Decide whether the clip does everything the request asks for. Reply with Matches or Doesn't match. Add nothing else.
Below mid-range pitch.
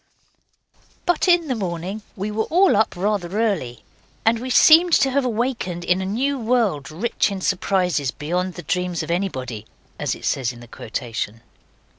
Doesn't match